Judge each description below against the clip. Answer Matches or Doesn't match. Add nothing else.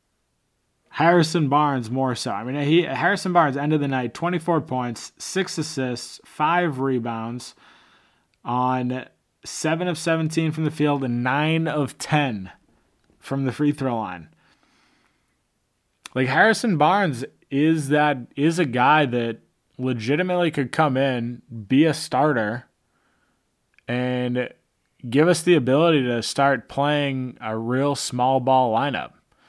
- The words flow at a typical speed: Doesn't match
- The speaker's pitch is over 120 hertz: Matches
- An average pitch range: Matches